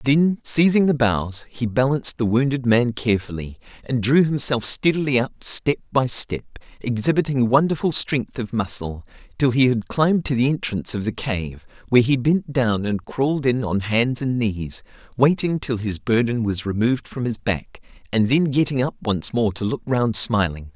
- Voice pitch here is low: Yes, low, 120 Hz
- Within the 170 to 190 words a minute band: Yes, average, 180 wpm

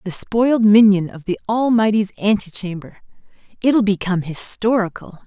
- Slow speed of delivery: Yes, slow, 125 wpm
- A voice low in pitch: No, high, 205 Hz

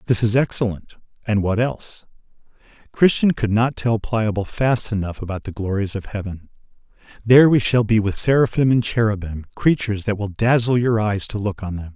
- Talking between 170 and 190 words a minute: Yes, average, 180 wpm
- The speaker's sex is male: Yes, male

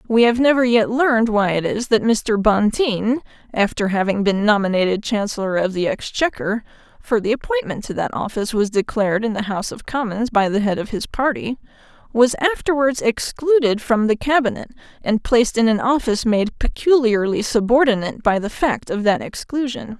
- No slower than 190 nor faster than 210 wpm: No, average, 170 wpm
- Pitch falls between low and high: No, high, 225 Hz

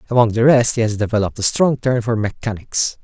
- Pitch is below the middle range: Yes, low, 115 Hz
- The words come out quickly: Yes, fast, 215 wpm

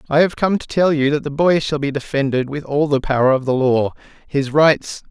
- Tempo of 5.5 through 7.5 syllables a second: No, 5.3 syllables/s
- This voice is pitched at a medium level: Yes, medium, 145 Hz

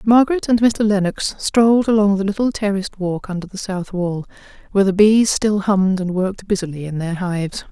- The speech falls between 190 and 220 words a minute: Yes, average, 195 wpm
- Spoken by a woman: Yes, female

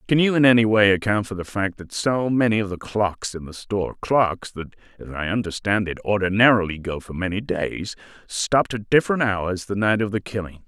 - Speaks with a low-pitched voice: Yes, low, 105 Hz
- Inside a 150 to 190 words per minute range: No, average, 200 wpm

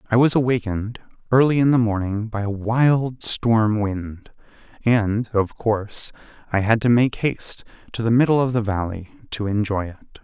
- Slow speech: No, average, 170 wpm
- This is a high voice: No, low, 110 Hz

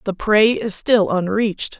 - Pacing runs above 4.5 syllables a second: No, 4.2 syllables/s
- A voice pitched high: Yes, high, 210 Hz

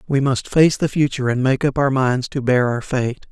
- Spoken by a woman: No, male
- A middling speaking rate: No, fast, 255 wpm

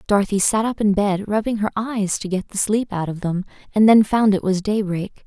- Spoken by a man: No, female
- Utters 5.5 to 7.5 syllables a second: No, 5.3 syllables/s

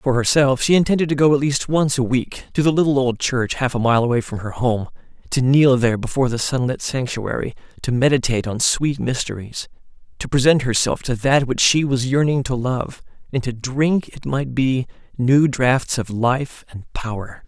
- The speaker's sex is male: Yes, male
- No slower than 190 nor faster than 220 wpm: Yes, average, 200 wpm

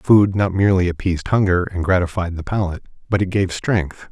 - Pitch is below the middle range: Yes, very low, 95 Hz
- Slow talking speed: No, average, 190 wpm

